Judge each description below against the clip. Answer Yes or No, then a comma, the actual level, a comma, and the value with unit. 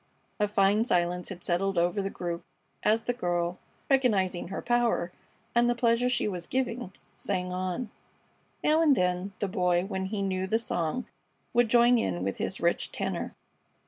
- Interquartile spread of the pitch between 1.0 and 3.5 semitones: No, average, 4.9 semitones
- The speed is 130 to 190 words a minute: Yes, average, 170 wpm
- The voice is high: Yes, high, 195 Hz